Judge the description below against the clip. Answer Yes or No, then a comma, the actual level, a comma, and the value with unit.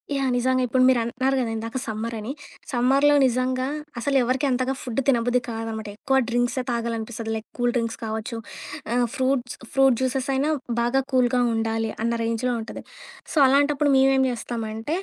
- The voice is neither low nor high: No, high, 245 Hz